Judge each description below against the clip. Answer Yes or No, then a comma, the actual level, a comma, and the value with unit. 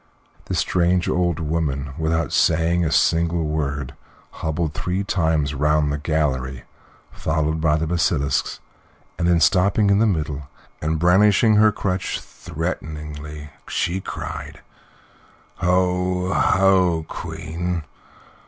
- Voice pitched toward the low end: Yes, very low, 80 Hz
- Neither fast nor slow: No, slow, 110 wpm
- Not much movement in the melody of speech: No, average, 3.1 semitones